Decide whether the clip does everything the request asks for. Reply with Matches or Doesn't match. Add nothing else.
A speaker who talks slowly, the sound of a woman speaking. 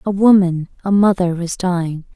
Doesn't match